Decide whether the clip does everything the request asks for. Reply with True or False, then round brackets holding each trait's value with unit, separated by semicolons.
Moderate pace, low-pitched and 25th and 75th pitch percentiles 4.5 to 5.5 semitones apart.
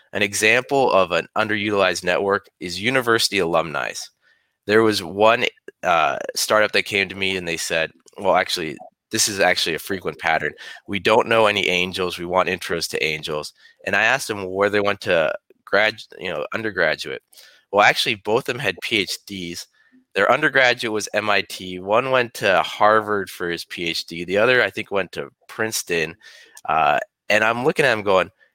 True (175 wpm; 105 Hz; 4.9 semitones)